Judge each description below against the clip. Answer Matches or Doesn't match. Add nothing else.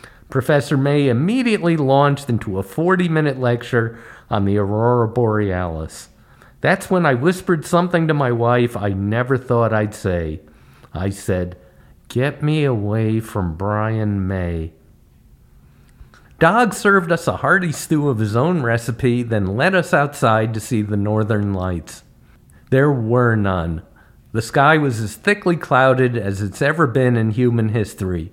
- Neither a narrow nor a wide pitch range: Doesn't match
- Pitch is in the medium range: Doesn't match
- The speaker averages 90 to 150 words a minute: Matches